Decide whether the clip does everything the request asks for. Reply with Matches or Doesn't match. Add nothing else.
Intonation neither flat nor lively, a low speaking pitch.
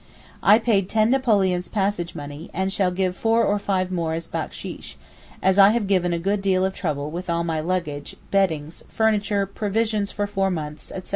Doesn't match